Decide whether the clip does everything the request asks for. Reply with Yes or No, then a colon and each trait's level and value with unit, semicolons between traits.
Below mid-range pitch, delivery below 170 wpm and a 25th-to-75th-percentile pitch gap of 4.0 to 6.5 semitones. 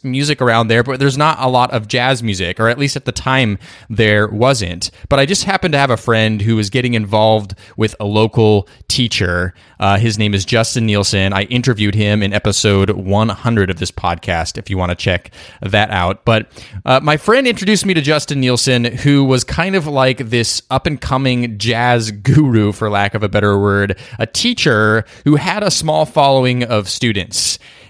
No: low, 115 Hz; average, 200 wpm; average, 4.3 semitones